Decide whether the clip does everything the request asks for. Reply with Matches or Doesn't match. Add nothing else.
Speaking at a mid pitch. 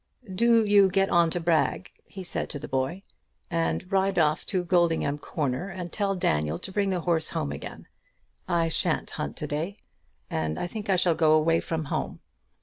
Matches